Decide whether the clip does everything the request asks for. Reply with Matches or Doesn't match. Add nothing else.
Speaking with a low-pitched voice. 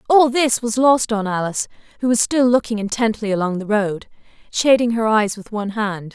Doesn't match